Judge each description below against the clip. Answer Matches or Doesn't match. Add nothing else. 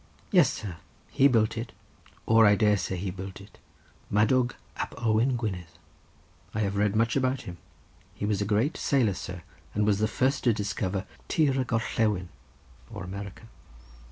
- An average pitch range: Matches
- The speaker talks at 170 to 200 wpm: Doesn't match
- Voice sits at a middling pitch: Doesn't match